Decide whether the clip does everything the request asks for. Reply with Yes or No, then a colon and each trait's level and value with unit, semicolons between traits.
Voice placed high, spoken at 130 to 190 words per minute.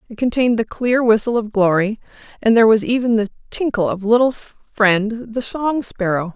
Yes: high, 225 Hz; average, 180 wpm